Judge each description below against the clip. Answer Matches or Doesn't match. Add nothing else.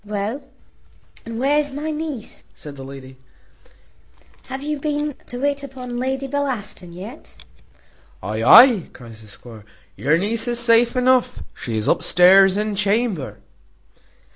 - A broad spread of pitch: Matches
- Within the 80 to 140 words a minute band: Matches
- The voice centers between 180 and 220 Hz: Doesn't match